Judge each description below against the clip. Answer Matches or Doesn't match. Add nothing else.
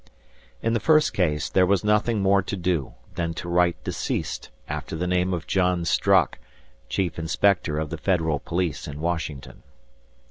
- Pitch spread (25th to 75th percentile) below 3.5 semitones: Matches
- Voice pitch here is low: Matches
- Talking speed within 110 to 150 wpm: Doesn't match